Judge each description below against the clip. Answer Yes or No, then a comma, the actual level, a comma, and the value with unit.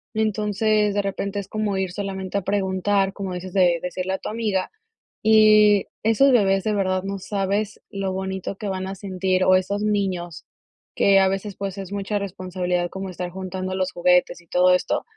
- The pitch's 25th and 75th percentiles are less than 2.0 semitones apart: Yes, narrow, 1.6 semitones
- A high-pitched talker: Yes, high, 195 Hz